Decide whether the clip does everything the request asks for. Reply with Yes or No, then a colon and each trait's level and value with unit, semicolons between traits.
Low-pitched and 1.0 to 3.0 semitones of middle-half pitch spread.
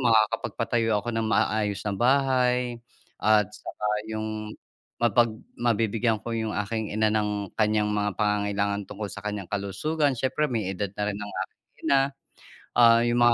Yes: low, 110 Hz; narrow, 2.5 semitones